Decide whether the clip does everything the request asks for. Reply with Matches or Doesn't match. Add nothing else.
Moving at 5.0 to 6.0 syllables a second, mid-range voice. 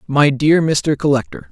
Doesn't match